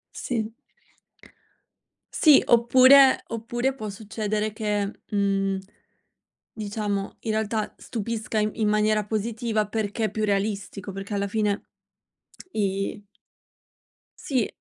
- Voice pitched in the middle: No, high, 215 Hz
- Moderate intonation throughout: No, narrow, 1.9 semitones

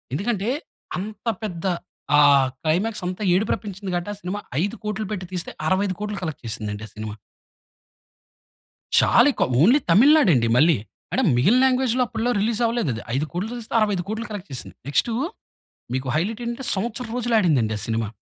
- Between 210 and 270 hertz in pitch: No, high, 200 Hz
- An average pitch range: No, wide, 6.2 semitones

